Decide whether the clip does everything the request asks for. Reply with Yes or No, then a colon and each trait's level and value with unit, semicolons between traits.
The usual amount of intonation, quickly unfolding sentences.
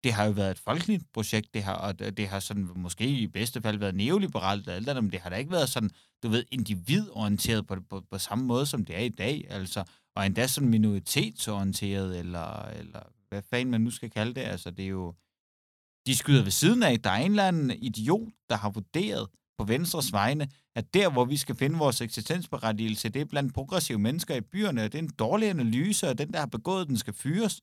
No: wide, 5.8 semitones; fast, 230 wpm